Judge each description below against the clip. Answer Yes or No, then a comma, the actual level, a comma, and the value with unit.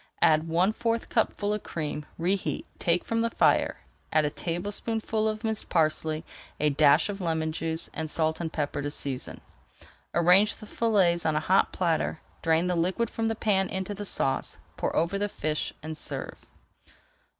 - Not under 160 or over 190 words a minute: Yes, average, 170 wpm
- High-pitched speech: No, medium, 170 Hz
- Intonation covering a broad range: No, average, 4.6 semitones